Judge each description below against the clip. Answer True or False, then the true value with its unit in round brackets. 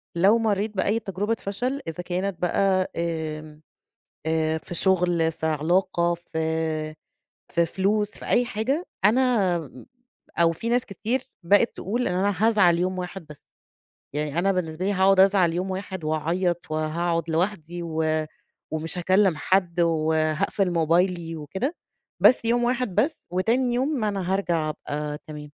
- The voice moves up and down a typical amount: True (3.9 semitones)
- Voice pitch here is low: False (180 Hz)